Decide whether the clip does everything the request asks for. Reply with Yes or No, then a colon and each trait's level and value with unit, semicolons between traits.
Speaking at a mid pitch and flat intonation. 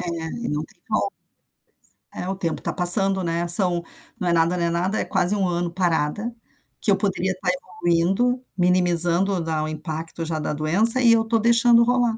No: medium, 180 Hz; average, 3.5 semitones